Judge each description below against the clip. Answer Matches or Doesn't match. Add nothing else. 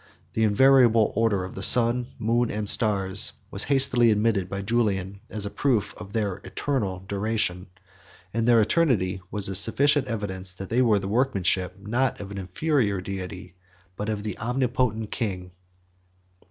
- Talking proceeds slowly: Doesn't match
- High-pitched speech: Doesn't match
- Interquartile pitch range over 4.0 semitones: Doesn't match